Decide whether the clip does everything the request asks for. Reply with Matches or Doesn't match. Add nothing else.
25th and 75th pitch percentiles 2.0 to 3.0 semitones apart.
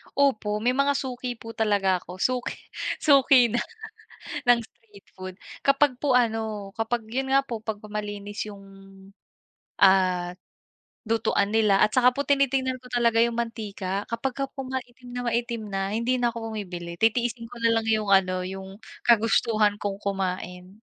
Doesn't match